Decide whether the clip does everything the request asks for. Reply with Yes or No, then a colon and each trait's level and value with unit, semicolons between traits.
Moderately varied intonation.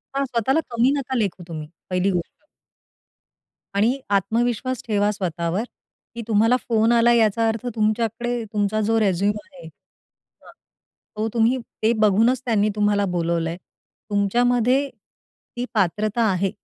Yes: average, 3.0 semitones